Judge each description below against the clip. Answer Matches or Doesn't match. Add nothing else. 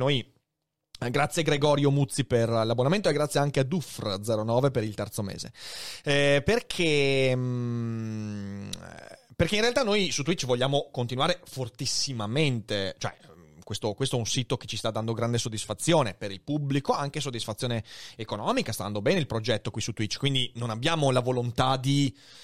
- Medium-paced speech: Matches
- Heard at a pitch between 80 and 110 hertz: Doesn't match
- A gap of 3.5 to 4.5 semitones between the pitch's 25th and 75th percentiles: Matches